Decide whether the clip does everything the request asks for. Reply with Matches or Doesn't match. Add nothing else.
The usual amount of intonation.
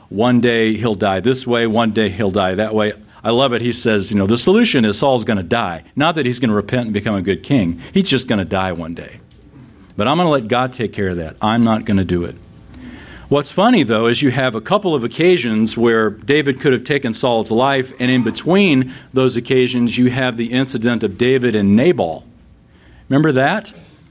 Matches